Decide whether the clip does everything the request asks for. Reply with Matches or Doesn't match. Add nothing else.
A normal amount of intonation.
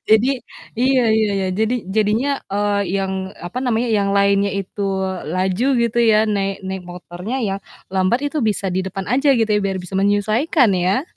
Matches